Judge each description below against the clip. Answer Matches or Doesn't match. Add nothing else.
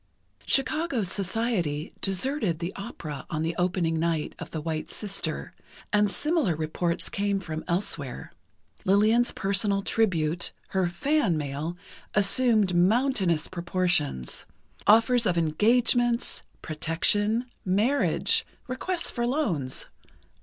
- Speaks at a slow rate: Matches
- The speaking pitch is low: Doesn't match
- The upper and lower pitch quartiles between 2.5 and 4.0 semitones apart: Doesn't match